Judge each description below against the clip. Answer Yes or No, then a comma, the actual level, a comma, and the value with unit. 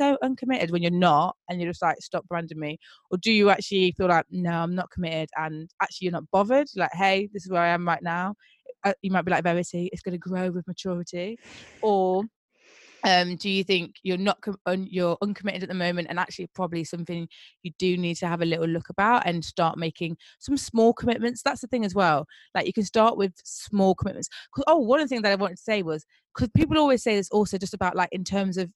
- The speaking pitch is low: No, medium, 185 Hz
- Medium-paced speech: No, fast, 240 wpm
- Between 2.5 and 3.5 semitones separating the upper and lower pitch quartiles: Yes, average, 2.8 semitones